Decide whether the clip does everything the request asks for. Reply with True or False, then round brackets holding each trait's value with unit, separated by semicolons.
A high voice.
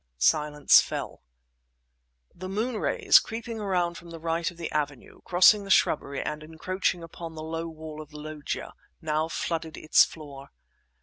False (165 Hz)